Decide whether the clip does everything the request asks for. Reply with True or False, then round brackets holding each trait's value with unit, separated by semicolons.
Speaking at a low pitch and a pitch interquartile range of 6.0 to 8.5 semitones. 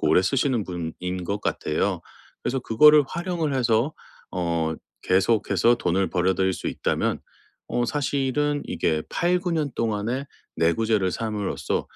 True (115 Hz; 7.2 semitones)